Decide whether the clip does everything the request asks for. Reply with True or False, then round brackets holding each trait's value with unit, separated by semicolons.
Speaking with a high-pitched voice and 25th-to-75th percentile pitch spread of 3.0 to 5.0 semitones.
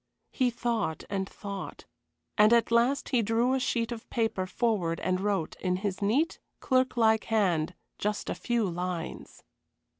True (220 Hz; 4.1 semitones)